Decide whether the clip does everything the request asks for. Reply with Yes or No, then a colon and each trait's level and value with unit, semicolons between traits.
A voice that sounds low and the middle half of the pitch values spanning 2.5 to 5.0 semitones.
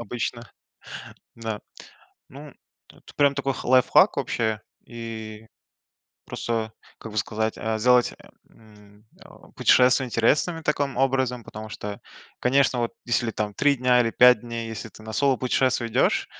Yes: low, 120 Hz; average, 2.8 semitones